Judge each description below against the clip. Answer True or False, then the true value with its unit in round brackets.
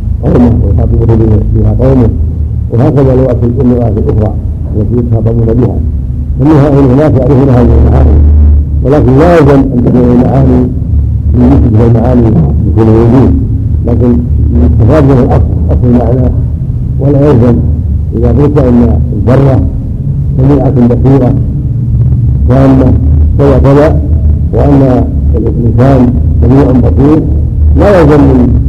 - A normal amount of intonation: False (7.6 semitones)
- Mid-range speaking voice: False (115 Hz)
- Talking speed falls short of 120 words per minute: True (100 wpm)